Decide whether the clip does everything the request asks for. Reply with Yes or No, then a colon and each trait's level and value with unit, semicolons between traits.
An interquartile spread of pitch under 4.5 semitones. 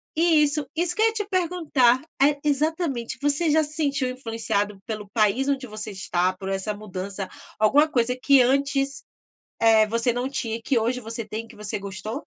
No: average, 5.2 semitones